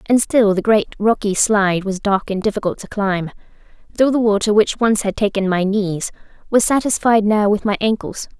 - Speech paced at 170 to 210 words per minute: Yes, average, 195 wpm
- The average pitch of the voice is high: Yes, high, 210 Hz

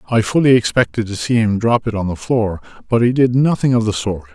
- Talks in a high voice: No, low, 115 Hz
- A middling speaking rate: No, fast, 250 wpm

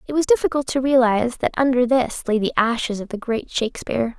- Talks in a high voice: Yes, very high, 250 Hz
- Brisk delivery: Yes, fast, 215 wpm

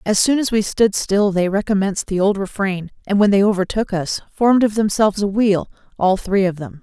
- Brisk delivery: Yes, fast, 220 wpm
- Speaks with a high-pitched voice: Yes, high, 200 Hz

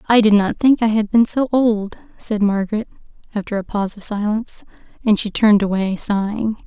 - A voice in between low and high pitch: No, high, 210 Hz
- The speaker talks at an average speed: Yes, average, 190 wpm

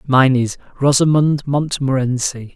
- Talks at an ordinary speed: No, slow, 95 wpm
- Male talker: Yes, male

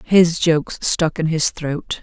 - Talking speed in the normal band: Yes, average, 180 wpm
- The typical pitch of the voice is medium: Yes, medium, 160 Hz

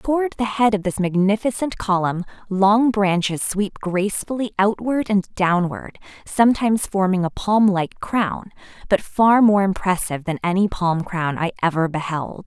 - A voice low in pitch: No, high, 195 Hz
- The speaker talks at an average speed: Yes, average, 150 wpm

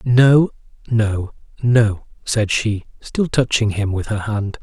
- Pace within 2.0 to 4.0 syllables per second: Yes, 3.4 syllables/s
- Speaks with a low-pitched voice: Yes, low, 110 Hz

